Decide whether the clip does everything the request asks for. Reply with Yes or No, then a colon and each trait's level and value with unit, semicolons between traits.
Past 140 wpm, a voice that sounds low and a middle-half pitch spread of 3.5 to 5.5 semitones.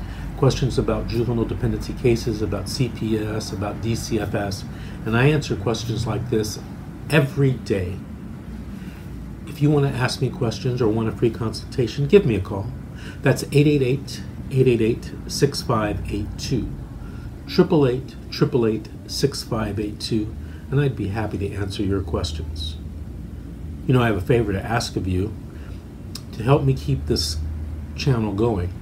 No: slow, 135 wpm; low, 110 Hz; average, 4.0 semitones